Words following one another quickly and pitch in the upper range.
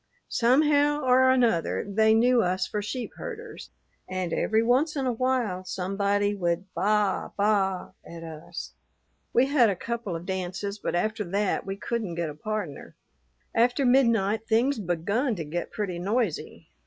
No: average, 155 wpm; high, 210 Hz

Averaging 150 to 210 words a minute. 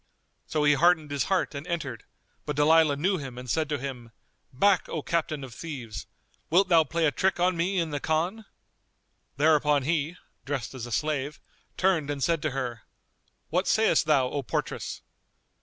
Yes: average, 175 wpm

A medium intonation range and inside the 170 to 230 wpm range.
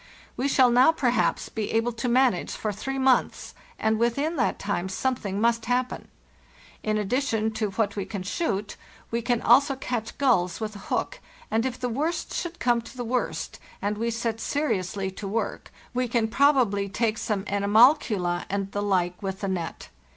Yes: average, 3.8 semitones; average, 180 wpm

